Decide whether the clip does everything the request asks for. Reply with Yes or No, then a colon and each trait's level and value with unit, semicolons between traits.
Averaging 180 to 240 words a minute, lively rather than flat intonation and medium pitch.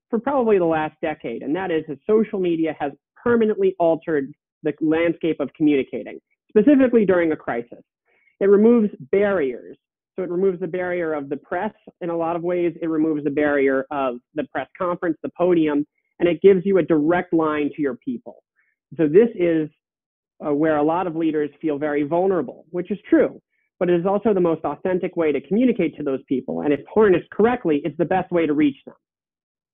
No: average, 195 wpm; average, 4.3 semitones; medium, 165 Hz